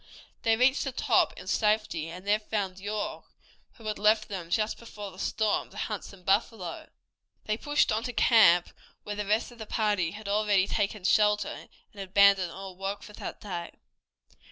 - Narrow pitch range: Yes, narrow, 2.1 semitones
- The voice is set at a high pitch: Yes, high, 210 Hz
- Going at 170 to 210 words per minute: Yes, average, 185 wpm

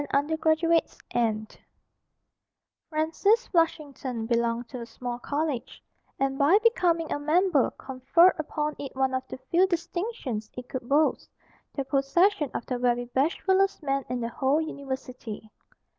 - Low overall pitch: No, very high, 280 Hz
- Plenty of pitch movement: No, average, 4.7 semitones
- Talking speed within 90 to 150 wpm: Yes, average, 140 wpm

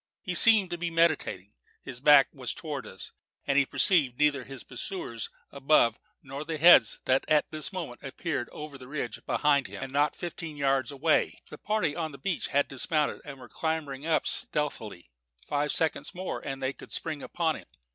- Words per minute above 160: Yes, average, 185 wpm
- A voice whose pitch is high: No, medium, 145 Hz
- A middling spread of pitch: Yes, average, 3.1 semitones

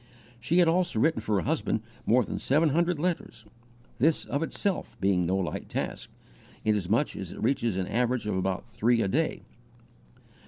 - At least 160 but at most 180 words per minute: Yes, average, 170 wpm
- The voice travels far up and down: Yes, wide, 7.6 semitones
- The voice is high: No, low, 120 Hz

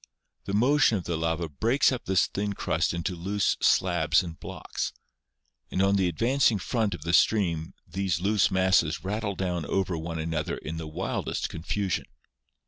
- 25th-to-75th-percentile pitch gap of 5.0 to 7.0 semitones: No, average, 3.7 semitones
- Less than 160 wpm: No, average, 165 wpm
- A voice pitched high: No, very low, 95 Hz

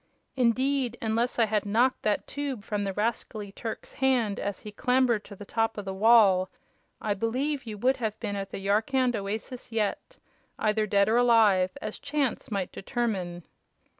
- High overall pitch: Yes, high, 220 Hz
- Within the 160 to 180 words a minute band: Yes, average, 170 wpm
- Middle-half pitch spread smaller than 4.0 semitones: Yes, average, 3.3 semitones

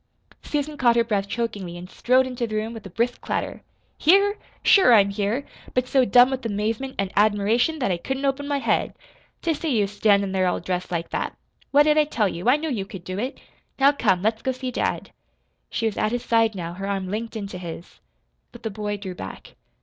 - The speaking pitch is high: Yes, high, 225 Hz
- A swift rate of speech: Yes, fast, 220 wpm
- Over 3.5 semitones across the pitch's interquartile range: Yes, average, 4.8 semitones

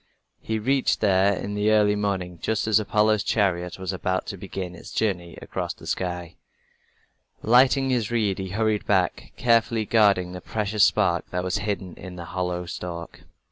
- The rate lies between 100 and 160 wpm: No, average, 170 wpm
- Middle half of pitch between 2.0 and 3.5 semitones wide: Yes, average, 3.1 semitones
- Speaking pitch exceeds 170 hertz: No, low, 100 Hz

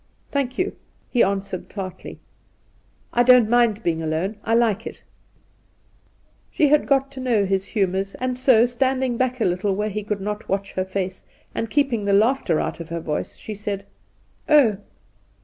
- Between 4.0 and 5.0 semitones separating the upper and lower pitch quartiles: Yes, average, 4.5 semitones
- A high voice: Yes, high, 215 Hz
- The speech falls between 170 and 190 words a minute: Yes, average, 180 wpm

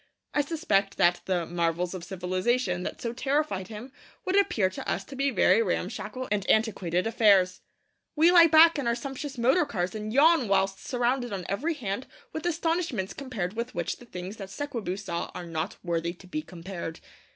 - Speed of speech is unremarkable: Yes, average, 185 wpm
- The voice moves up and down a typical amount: No, wide, 6.7 semitones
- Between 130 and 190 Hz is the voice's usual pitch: No, high, 215 Hz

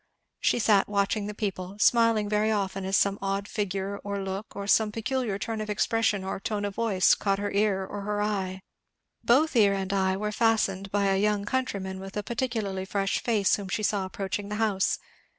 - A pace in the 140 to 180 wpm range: No, average, 200 wpm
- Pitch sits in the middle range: No, high, 200 Hz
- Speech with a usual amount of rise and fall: No, narrow, 1.7 semitones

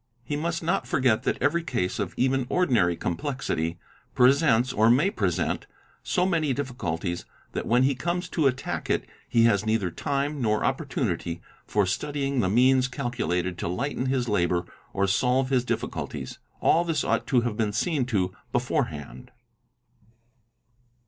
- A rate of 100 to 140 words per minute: No, average, 150 wpm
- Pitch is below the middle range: Yes, low, 125 Hz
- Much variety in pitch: Yes, wide, 5.7 semitones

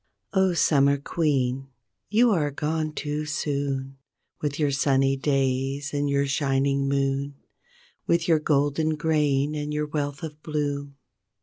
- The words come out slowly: Yes, slow, 130 wpm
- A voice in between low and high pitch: Yes, medium, 145 Hz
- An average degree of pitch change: No, narrow, 1.8 semitones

